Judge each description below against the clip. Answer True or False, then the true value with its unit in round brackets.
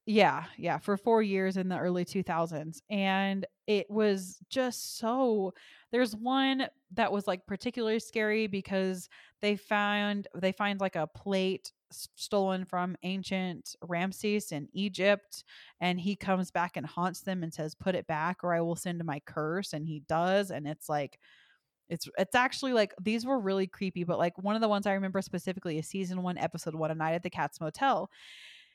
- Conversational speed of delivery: True (185 wpm)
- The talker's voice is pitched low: False (190 Hz)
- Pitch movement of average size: True (3.1 semitones)